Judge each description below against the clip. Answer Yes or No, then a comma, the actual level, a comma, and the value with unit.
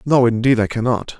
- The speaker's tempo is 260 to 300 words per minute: No, average, 200 wpm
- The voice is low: Yes, low, 120 Hz